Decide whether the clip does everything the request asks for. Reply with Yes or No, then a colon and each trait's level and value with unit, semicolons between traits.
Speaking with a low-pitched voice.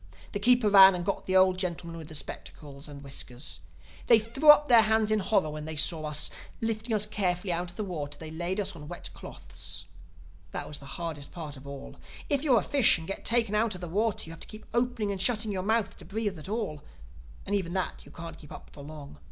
No: medium, 185 Hz